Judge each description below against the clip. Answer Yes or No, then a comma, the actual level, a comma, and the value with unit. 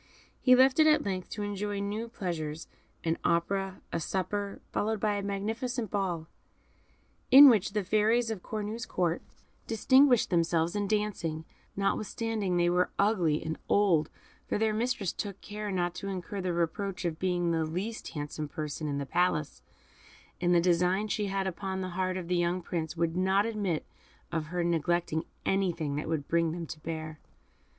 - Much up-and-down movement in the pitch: No, average, 3.7 semitones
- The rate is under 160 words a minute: No, average, 170 wpm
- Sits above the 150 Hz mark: Yes, medium, 185 Hz